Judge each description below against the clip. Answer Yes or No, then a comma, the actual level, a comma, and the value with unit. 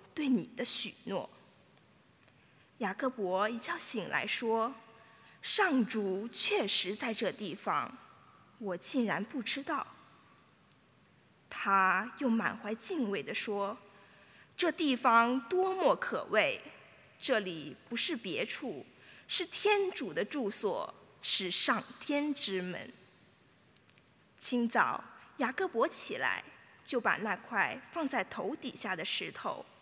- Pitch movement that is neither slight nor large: No, wide, 6.1 semitones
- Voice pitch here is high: Yes, high, 235 Hz